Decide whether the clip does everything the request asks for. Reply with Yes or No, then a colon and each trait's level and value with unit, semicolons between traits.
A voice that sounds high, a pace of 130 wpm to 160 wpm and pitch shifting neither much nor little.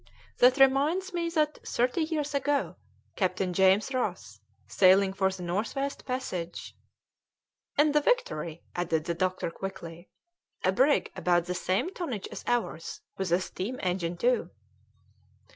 No: high, 195 Hz; average, 145 wpm; wide, 7.6 semitones